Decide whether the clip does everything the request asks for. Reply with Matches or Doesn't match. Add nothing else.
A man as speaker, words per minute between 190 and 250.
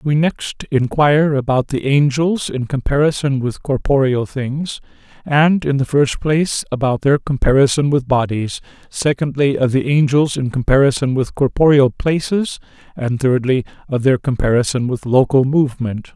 Doesn't match